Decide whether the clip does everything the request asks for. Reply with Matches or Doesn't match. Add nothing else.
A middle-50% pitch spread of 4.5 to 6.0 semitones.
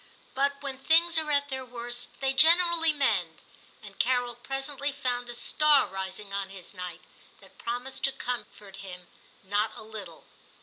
Matches